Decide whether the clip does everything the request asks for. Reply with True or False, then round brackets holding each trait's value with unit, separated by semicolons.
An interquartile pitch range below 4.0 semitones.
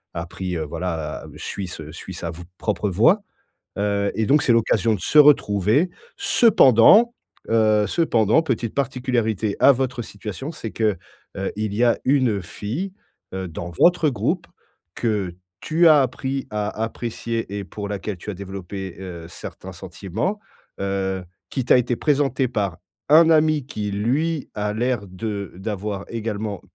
False (5.2 semitones)